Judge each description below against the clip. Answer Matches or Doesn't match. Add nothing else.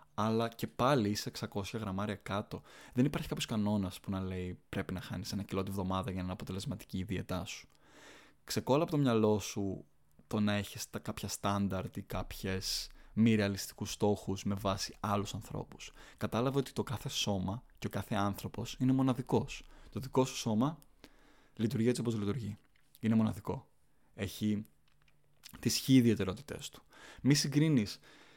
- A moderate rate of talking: Matches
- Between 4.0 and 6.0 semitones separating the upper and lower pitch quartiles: Doesn't match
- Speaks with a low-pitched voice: Matches